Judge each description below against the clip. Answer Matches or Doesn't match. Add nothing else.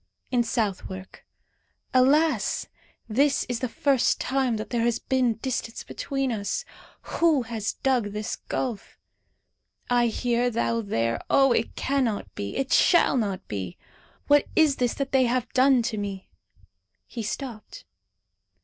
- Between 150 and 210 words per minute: Doesn't match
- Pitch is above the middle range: Matches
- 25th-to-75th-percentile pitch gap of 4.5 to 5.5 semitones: Doesn't match